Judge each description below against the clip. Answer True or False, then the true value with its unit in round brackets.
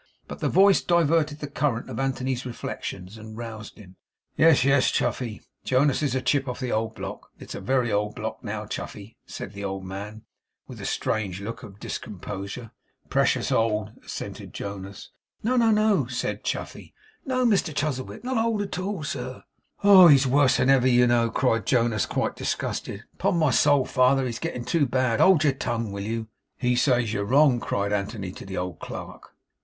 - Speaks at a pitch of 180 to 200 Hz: False (125 Hz)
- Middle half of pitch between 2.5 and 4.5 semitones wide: False (5.2 semitones)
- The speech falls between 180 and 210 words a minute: True (185 wpm)